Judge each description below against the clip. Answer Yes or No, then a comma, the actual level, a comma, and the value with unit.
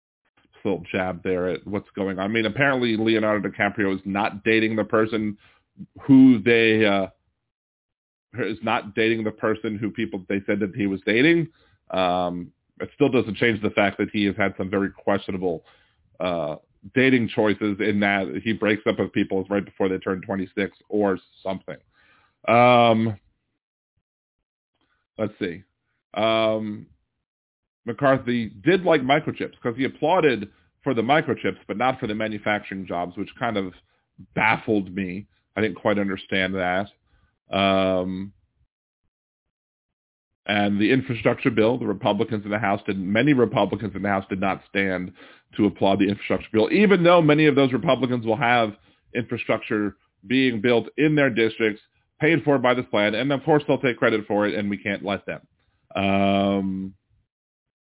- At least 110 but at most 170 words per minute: Yes, average, 160 wpm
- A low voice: Yes, low, 105 Hz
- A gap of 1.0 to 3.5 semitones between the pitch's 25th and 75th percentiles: Yes, average, 2.7 semitones